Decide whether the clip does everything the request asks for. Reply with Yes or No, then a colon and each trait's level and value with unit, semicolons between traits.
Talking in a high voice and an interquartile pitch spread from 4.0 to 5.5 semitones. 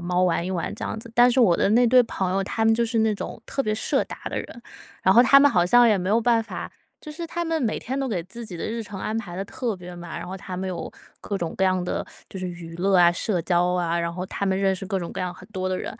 Yes: high, 195 Hz; average, 4.3 semitones